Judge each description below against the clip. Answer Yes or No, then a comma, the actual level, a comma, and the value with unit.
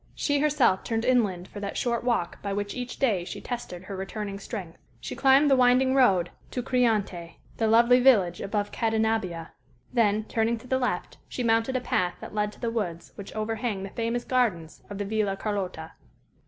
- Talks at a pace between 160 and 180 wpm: No, average, 190 wpm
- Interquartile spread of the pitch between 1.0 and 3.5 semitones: No, average, 4.0 semitones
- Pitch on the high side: Yes, high, 220 Hz